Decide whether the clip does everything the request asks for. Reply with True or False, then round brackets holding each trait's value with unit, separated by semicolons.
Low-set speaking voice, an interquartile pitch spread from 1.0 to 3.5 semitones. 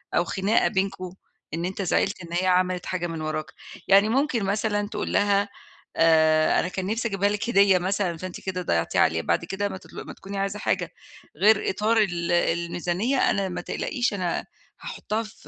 False (190 Hz; 2.9 semitones)